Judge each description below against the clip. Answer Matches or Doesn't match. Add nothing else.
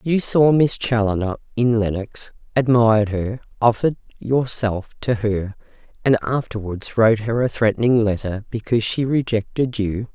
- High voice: Doesn't match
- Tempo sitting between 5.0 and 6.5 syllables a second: Doesn't match